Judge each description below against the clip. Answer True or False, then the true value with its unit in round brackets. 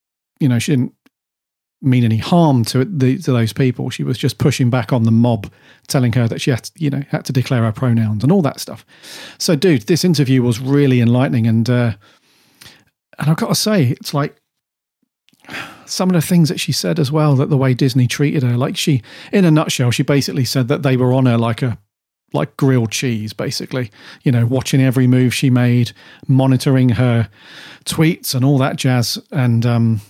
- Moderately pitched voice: False (130 Hz)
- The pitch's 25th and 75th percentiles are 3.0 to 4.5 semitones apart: True (3.3 semitones)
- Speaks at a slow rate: False (205 wpm)